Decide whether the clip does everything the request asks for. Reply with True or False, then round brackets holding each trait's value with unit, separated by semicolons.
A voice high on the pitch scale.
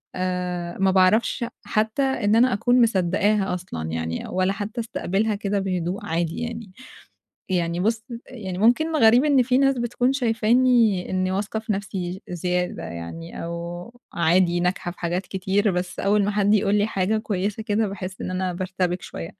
True (195 Hz)